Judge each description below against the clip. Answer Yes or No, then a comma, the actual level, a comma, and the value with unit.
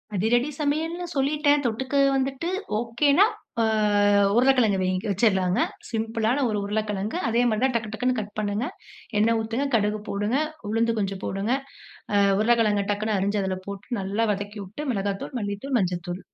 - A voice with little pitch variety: No, average, 3.8 semitones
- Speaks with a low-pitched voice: No, high, 220 Hz